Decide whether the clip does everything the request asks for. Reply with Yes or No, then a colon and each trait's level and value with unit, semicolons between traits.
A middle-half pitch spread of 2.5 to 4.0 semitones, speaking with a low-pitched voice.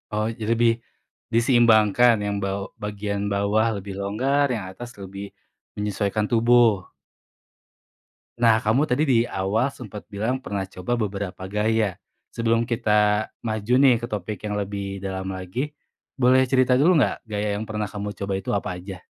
Yes: average, 2.8 semitones; low, 105 Hz